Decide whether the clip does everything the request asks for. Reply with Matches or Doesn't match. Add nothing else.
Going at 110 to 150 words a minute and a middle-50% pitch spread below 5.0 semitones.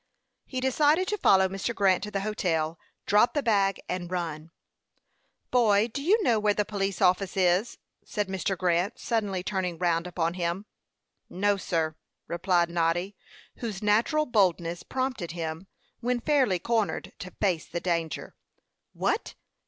Matches